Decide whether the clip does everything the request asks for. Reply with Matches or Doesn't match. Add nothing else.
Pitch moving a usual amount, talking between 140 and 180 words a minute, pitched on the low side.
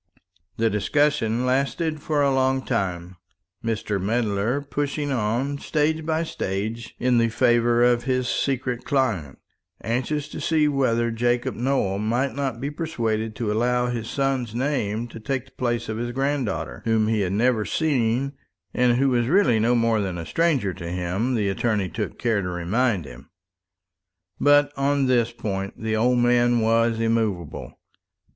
Matches